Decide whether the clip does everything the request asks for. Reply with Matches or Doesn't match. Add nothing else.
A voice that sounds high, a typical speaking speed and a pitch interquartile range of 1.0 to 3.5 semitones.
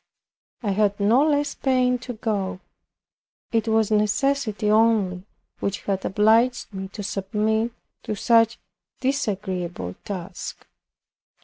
Doesn't match